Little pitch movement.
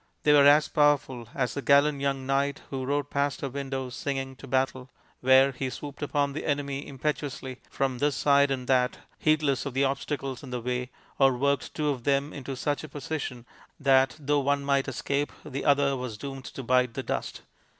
Yes: narrow, 1.5 semitones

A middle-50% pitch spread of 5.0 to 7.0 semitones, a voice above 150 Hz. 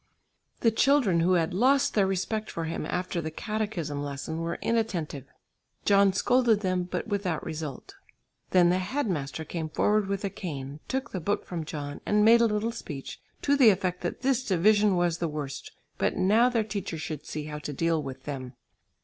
Yes: average, 5.3 semitones; medium, 185 Hz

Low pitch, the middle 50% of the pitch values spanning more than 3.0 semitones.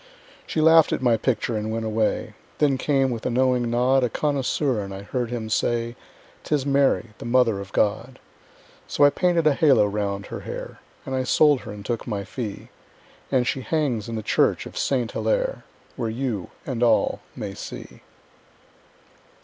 Yes: low, 120 Hz; average, 3.7 semitones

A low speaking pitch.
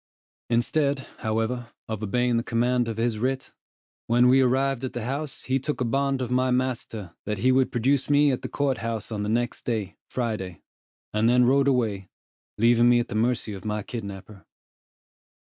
Yes: low, 120 Hz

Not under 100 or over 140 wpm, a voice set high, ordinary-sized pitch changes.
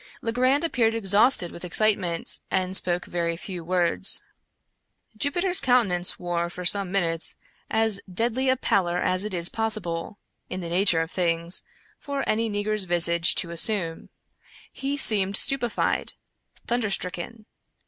Yes: slow, 135 wpm; high, 195 Hz; average, 4.6 semitones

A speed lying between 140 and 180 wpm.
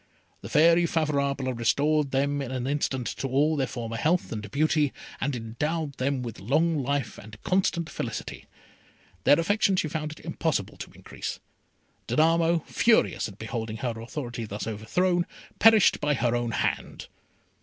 Yes: average, 155 wpm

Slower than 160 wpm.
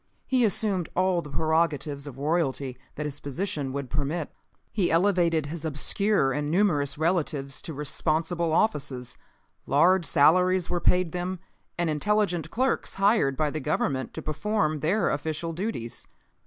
Yes: average, 140 wpm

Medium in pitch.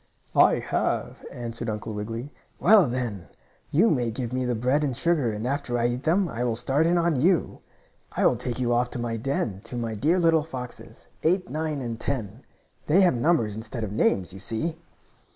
No: low, 125 Hz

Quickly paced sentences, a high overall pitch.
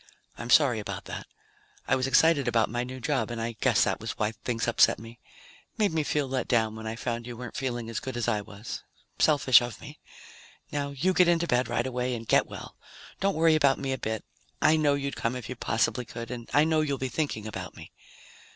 No: fast, 230 wpm; low, 125 Hz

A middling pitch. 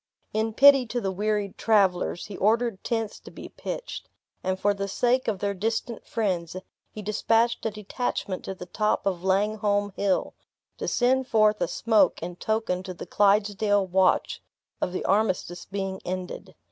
No: high, 205 Hz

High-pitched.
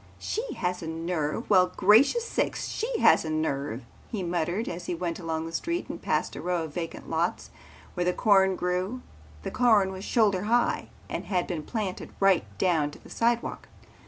No: medium, 180 Hz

